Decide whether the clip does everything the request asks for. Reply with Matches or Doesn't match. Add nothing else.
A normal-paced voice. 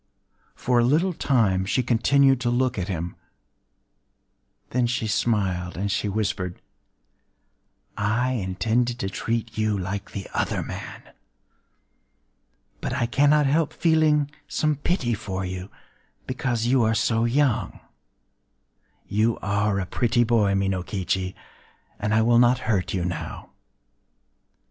Doesn't match